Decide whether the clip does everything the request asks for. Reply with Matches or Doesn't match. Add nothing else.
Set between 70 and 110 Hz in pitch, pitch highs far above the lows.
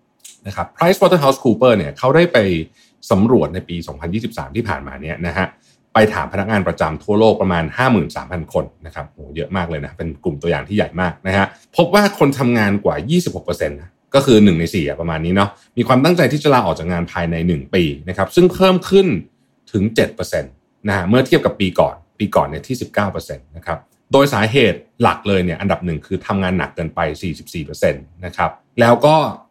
Matches